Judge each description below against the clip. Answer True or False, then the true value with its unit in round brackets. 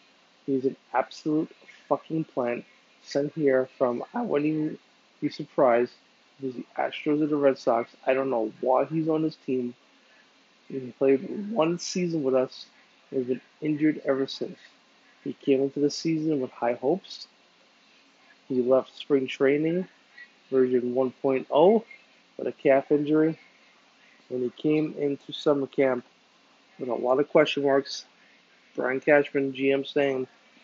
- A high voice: False (140 Hz)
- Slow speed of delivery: False (145 wpm)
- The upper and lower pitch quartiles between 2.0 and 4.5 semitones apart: True (2.8 semitones)